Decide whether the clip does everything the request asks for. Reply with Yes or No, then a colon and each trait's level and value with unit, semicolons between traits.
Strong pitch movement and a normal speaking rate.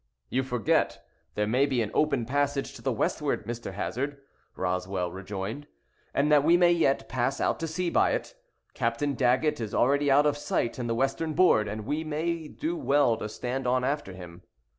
No: average, 4.9 semitones; average, 190 wpm